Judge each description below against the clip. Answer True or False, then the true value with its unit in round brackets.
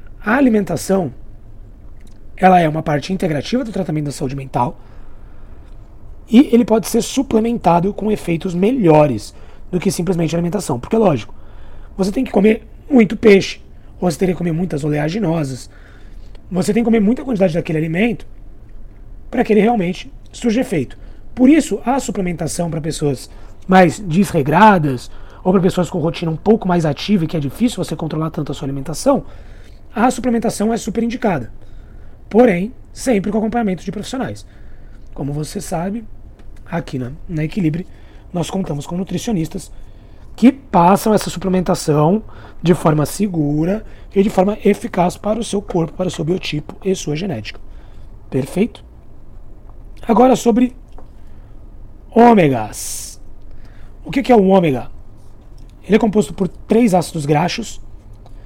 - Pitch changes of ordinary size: False (6.8 semitones)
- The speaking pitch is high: False (175 Hz)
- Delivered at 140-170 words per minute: True (145 wpm)